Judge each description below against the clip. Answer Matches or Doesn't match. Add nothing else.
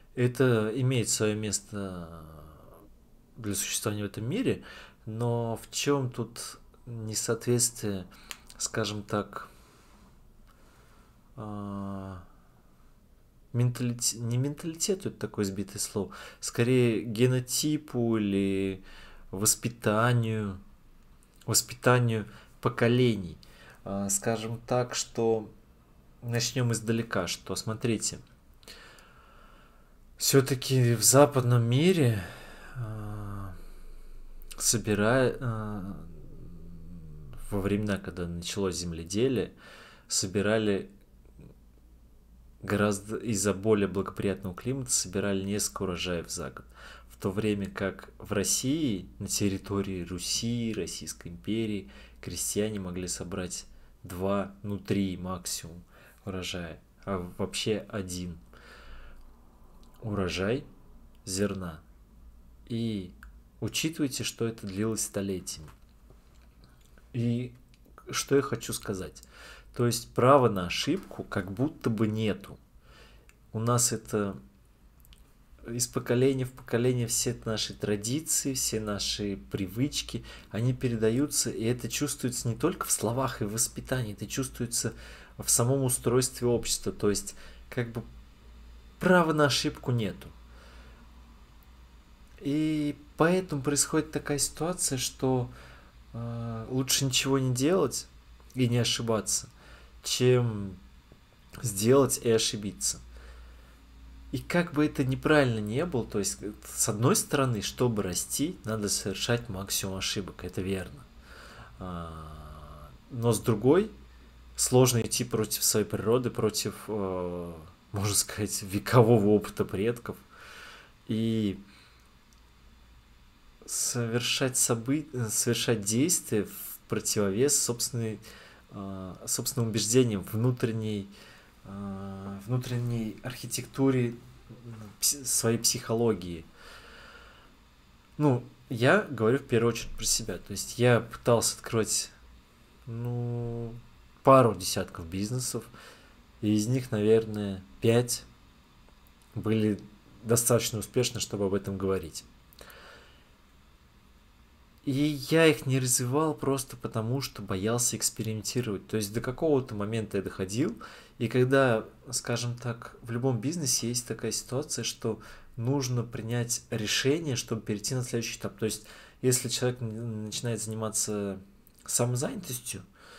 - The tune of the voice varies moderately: Matches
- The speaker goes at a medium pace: Doesn't match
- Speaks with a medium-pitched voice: Doesn't match